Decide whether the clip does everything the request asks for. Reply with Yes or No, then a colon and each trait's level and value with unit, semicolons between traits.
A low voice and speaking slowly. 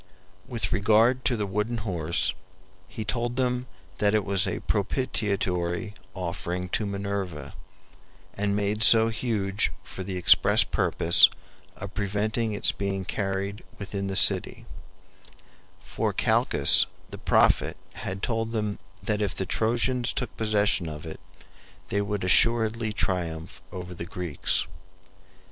Yes: low, 100 Hz; slow, 130 wpm